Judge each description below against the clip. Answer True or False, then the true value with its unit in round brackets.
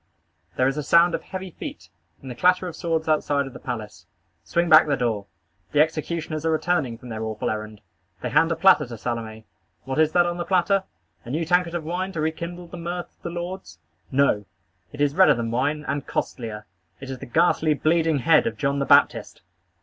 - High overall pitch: False (155 Hz)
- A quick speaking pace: True (210 wpm)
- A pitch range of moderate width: False (5.7 semitones)